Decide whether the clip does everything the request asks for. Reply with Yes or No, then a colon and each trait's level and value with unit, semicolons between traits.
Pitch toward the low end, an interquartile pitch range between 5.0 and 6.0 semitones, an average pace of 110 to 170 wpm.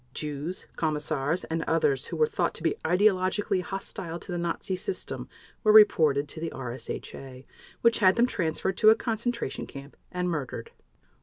No: medium, 175 Hz; wide, 5.6 semitones; average, 160 wpm